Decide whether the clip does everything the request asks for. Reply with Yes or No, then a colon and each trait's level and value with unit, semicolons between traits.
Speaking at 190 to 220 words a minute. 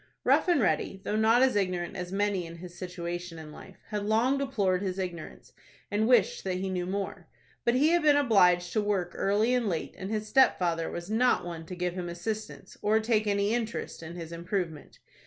Yes: fast, 205 wpm